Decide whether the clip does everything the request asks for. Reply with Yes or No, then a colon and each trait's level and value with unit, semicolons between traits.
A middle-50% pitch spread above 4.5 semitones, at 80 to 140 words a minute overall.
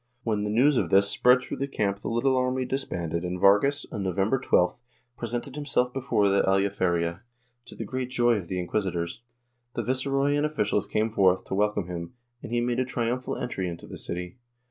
No: average, 5.1 semitones; average, 200 wpm